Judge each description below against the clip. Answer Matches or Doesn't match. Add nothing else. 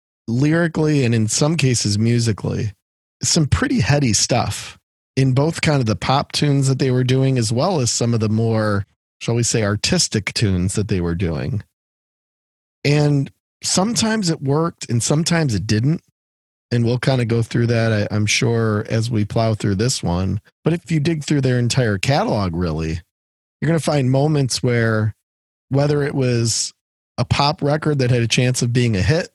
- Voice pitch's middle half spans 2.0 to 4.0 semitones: Doesn't match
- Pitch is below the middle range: Matches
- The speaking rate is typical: Matches